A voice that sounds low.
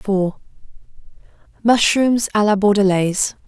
No: high, 205 Hz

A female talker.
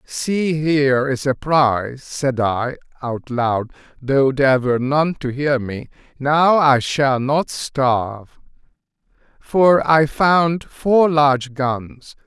No: male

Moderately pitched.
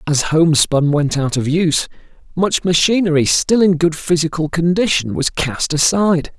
Yes: medium, 165 Hz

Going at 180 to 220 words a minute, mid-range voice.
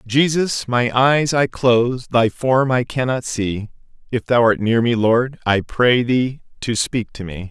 No: average, 185 wpm; low, 120 Hz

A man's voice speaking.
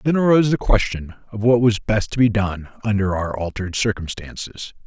Yes: male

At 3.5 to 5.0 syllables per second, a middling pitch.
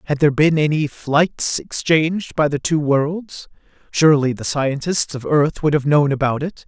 Yes: 4.6 syllables/s; medium, 150 Hz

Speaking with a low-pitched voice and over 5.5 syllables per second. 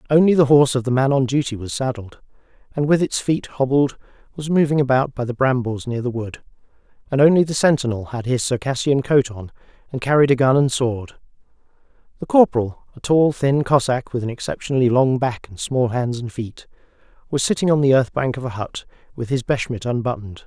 Yes: low, 130 Hz; 5.7 syllables/s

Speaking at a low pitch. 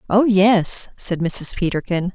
No: high, 190 Hz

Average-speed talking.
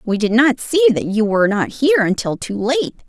No: fast, 235 wpm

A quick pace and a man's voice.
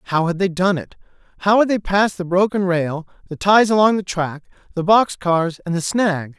Yes: fast, 215 wpm; male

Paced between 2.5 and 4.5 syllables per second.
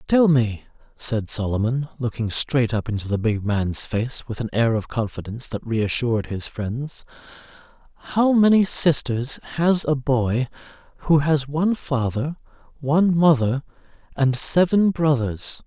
Yes: 4.3 syllables/s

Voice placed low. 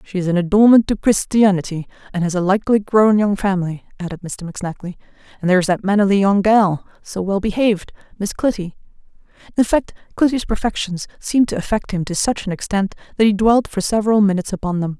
No: high, 200 Hz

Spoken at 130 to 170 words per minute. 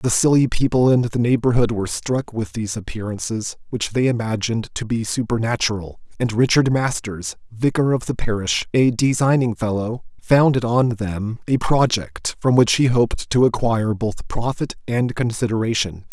Yes: average, 155 wpm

